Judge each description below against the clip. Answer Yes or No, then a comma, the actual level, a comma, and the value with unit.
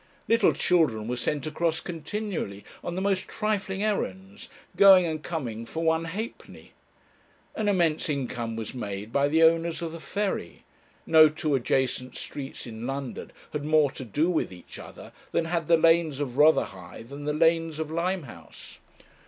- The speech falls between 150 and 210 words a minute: Yes, average, 160 wpm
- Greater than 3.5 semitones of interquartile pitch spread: Yes, average, 4.5 semitones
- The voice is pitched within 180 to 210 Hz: No, medium, 155 Hz